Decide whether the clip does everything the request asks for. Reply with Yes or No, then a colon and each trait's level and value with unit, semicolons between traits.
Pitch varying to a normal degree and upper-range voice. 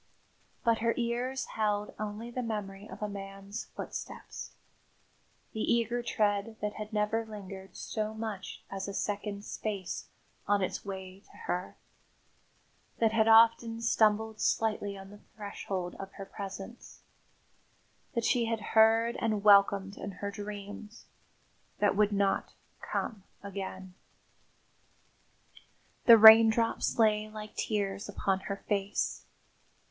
No: narrow, 2.0 semitones; high, 210 Hz